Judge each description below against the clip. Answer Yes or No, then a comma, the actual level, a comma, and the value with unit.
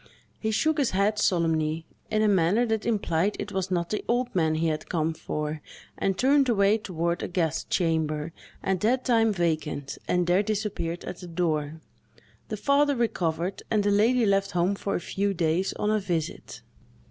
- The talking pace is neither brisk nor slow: Yes, average, 180 wpm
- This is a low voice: No, high, 190 Hz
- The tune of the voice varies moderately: Yes, average, 4.7 semitones